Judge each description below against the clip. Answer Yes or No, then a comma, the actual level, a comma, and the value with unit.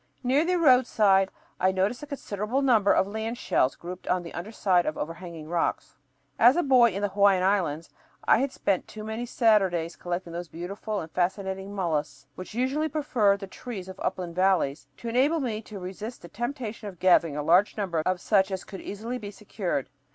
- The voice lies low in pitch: No, high, 200 Hz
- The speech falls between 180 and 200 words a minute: Yes, average, 195 wpm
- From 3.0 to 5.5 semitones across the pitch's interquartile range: Yes, average, 4.4 semitones